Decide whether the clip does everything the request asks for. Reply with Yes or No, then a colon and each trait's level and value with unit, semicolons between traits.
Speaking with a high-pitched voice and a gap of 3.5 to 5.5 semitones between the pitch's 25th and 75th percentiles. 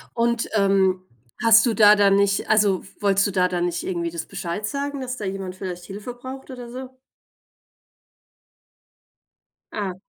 Yes: high, 200 Hz; average, 4.0 semitones